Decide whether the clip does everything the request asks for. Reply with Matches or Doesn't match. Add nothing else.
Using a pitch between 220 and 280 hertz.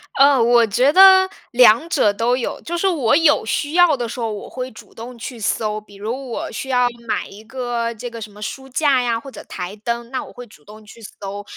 Matches